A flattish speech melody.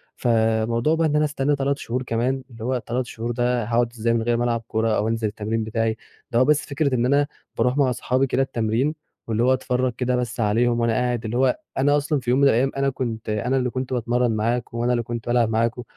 Yes: narrow, 2.3 semitones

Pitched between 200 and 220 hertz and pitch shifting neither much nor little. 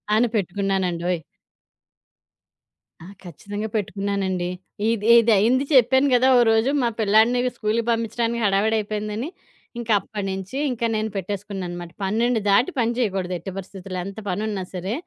Yes: high, 210 Hz; average, 3.2 semitones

